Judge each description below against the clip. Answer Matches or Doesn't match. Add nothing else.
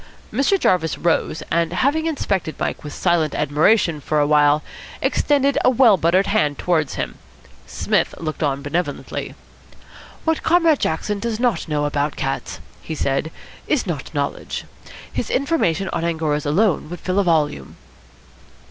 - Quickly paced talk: Doesn't match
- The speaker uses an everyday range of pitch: Doesn't match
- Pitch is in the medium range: Matches